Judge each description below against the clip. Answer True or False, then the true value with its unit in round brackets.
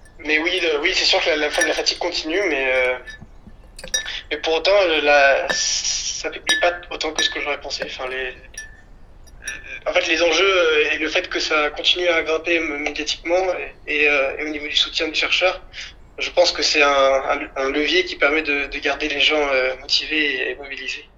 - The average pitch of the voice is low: False (150 Hz)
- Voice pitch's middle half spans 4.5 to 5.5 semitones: False (3.4 semitones)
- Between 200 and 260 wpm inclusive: True (205 wpm)